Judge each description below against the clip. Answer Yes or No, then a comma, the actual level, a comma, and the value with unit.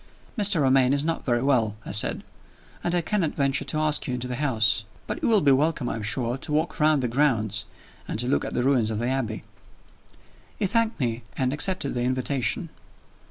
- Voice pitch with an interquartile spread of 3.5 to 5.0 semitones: Yes, average, 4.1 semitones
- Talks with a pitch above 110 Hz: Yes, low, 135 Hz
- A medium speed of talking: No, fast, 210 wpm